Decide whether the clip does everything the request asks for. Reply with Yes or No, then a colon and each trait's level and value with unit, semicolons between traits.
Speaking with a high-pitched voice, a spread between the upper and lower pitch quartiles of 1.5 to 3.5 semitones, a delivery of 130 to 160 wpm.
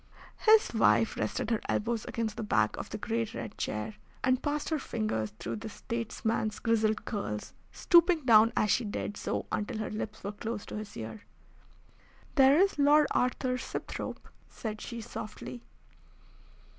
Yes: high, 225 Hz; average, 3.2 semitones; average, 155 wpm